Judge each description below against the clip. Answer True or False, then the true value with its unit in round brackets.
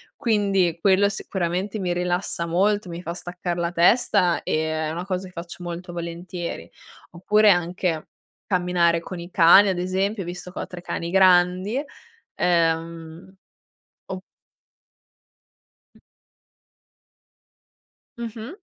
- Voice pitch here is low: False (180 Hz)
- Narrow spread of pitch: True (2.1 semitones)